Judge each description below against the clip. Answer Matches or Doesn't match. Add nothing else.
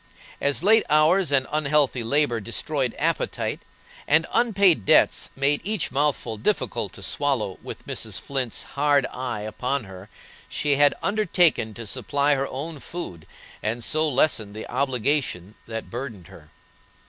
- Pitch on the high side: Doesn't match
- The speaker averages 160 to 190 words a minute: Doesn't match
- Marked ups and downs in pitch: Doesn't match